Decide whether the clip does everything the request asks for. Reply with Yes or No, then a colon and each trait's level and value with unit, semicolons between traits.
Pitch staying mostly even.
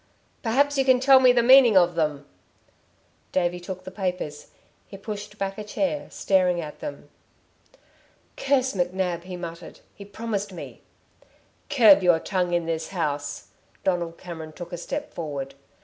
No: average, 4.7 semitones